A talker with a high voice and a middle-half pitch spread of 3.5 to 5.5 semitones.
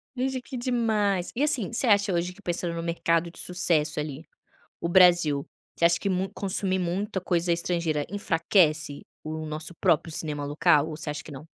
No: medium, 170 Hz; average, 3.8 semitones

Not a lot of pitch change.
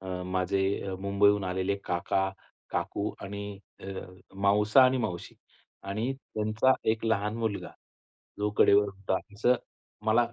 Yes: narrow, 1.9 semitones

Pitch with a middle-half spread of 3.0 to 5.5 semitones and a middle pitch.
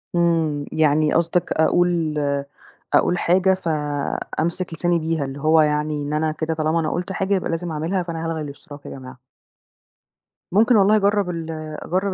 No: narrow, 2.6 semitones; medium, 165 Hz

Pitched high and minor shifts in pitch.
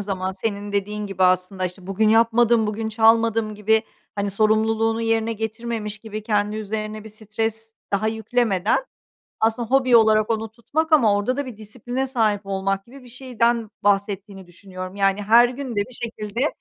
Yes: high, 220 Hz; narrow, 2.1 semitones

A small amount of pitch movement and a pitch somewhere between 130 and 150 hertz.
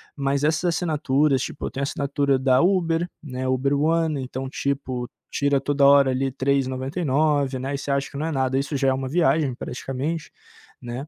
Yes: narrow, 2.2 semitones; medium, 140 Hz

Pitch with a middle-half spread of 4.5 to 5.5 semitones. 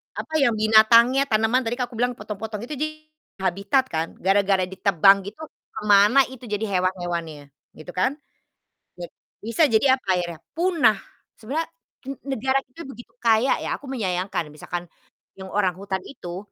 Yes: average, 5.2 semitones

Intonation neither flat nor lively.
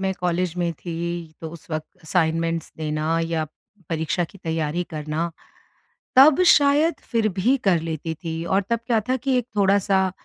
Yes: average, 3.7 semitones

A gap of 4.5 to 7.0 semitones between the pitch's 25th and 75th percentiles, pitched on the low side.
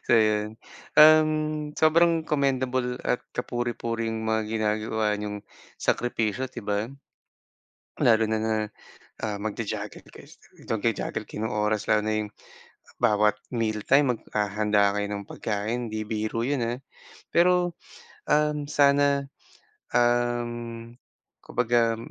No: average, 3.4 semitones; low, 115 Hz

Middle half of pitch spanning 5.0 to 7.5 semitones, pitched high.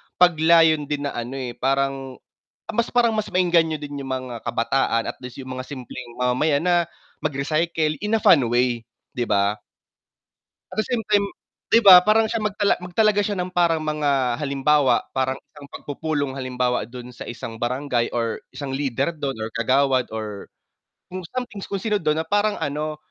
No: wide, 5.5 semitones; medium, 145 Hz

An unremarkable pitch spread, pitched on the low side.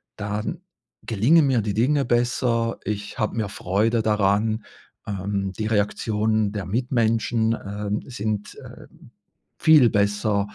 No: narrow, 2.1 semitones; low, 110 Hz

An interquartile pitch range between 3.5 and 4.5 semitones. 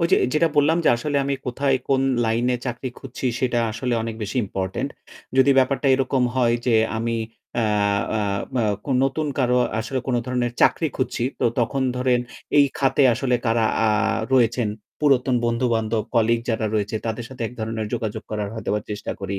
No: average, 2.8 semitones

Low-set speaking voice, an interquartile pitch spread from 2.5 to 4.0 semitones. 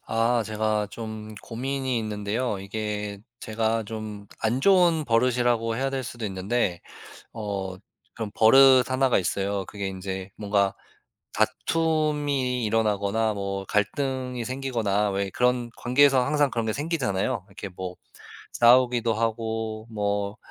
Yes: low, 110 Hz; average, 3.7 semitones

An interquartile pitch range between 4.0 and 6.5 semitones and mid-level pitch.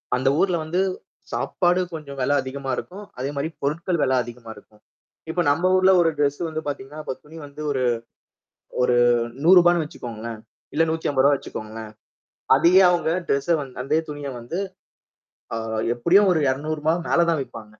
Yes: average, 4.3 semitones; medium, 145 Hz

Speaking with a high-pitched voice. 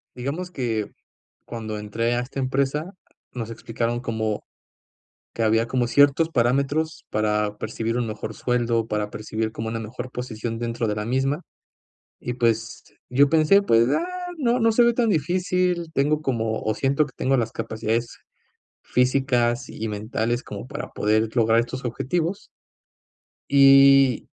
No: low, 120 Hz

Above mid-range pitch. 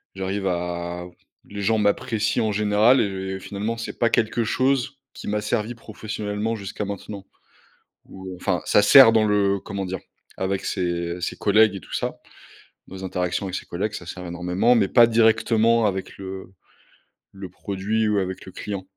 No: low, 100 Hz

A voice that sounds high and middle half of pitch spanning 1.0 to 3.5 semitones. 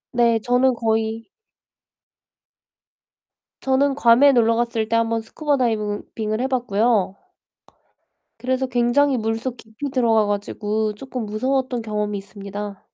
Yes: high, 230 Hz; average, 2.9 semitones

